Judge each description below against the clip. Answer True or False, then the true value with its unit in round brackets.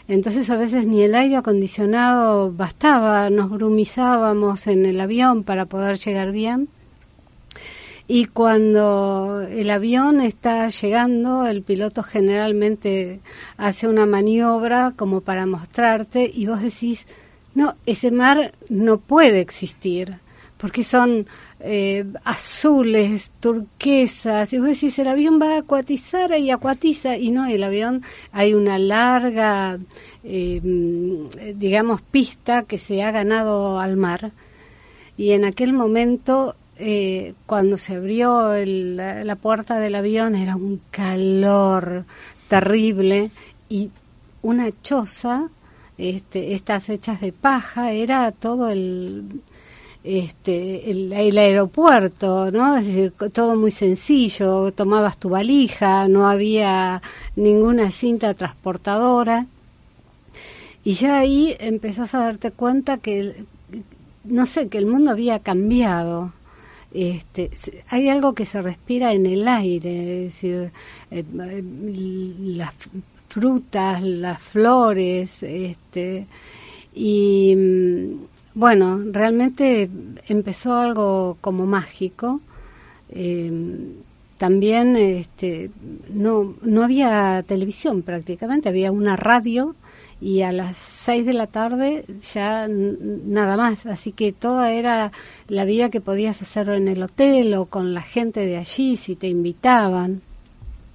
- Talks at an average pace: False (120 wpm)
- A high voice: True (210 Hz)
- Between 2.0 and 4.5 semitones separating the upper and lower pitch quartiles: True (3.8 semitones)